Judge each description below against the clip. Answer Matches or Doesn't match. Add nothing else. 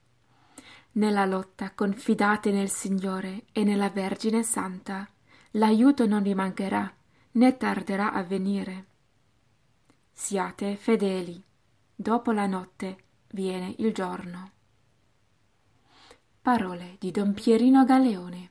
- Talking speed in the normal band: Doesn't match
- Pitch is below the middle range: Doesn't match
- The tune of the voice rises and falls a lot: Doesn't match